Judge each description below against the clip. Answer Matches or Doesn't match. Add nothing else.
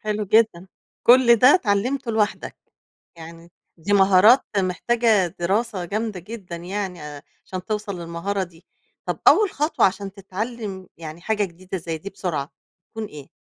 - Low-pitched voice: Doesn't match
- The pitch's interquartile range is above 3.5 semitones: Matches